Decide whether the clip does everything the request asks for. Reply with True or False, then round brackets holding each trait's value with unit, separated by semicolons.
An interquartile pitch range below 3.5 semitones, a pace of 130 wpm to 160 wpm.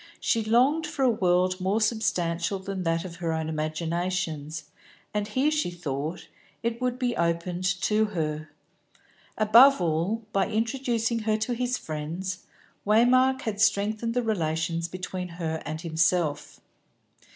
False (5.3 semitones; 140 wpm)